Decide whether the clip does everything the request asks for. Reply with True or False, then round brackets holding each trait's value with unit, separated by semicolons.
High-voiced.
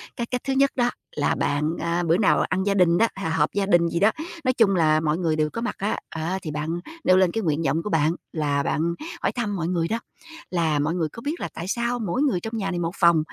False (175 Hz)